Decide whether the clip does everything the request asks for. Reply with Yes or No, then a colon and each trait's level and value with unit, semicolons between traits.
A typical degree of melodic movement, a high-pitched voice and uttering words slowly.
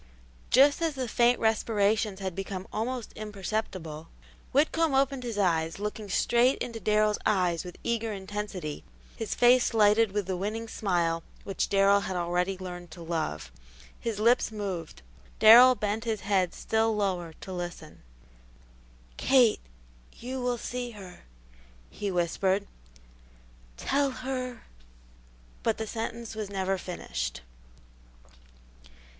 Yes: average, 4.2 semitones; high, 205 Hz; slow, 125 wpm